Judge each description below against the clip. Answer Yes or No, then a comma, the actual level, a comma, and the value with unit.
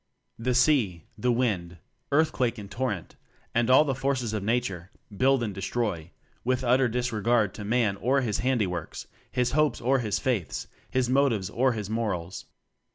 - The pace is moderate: Yes, average, 160 wpm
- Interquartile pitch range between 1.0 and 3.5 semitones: No, average, 3.9 semitones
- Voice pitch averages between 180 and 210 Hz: No, low, 120 Hz